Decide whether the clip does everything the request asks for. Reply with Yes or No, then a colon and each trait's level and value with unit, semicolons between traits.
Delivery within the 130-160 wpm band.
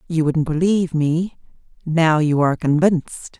Yes: average, 140 wpm